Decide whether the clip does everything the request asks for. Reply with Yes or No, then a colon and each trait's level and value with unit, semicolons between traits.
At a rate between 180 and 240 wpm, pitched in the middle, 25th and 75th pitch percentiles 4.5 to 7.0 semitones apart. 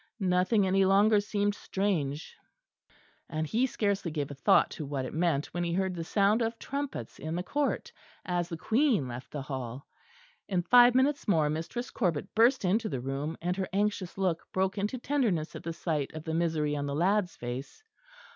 Yes: average, 190 wpm; medium, 180 Hz; average, 5.2 semitones